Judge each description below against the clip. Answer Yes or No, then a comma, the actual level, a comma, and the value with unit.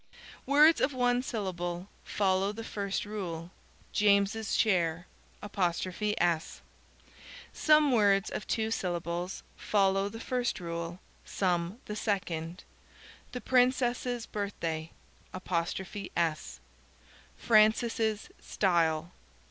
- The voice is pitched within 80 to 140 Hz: No, high, 200 Hz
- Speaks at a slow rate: Yes, slow, 85 wpm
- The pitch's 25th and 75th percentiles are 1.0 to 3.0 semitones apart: No, average, 4.4 semitones